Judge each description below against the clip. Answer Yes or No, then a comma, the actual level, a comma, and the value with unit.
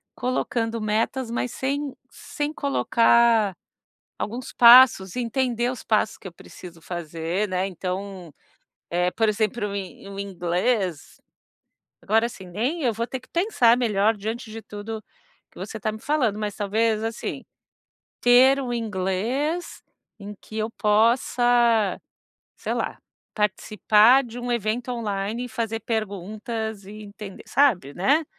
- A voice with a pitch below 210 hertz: No, high, 220 Hz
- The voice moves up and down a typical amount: Yes, average, 3.4 semitones